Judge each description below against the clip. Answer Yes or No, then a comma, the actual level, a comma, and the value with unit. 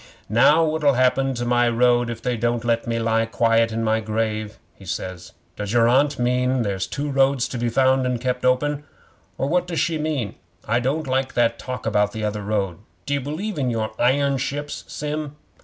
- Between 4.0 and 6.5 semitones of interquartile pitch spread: No, average, 3.5 semitones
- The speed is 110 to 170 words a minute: No, average, 195 wpm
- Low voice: Yes, low, 125 Hz